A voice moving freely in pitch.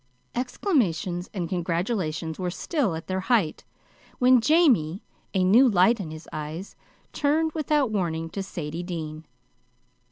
Yes: wide, 7.1 semitones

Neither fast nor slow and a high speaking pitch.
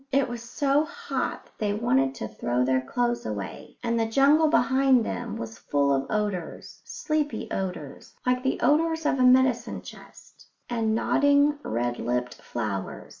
Yes: average, 160 wpm; high, 235 Hz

